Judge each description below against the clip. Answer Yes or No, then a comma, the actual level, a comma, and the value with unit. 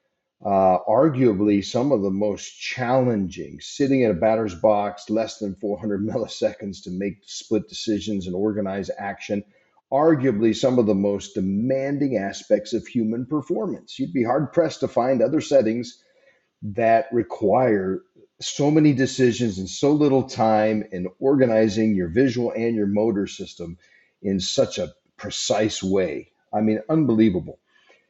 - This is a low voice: Yes, low, 110 Hz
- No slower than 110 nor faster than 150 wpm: Yes, average, 140 wpm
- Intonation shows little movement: No, average, 3.6 semitones